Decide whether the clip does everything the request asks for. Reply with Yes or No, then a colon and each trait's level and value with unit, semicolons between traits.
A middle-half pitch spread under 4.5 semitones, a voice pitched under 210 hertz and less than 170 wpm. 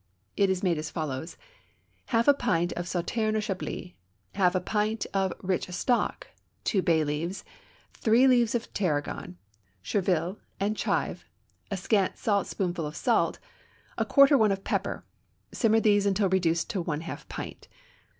Yes: average, 3.8 semitones; high, 190 Hz; average, 150 wpm